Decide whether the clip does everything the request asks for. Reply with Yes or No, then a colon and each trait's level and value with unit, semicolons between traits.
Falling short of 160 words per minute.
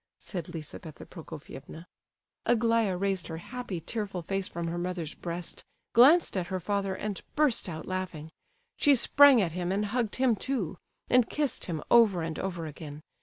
No: average, 165 wpm